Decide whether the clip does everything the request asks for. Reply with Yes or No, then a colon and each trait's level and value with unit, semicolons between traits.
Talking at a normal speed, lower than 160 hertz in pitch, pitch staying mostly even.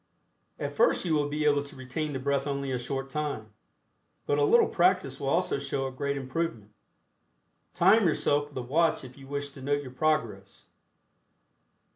Yes: average, 180 wpm; medium, 140 Hz; narrow, 2.3 semitones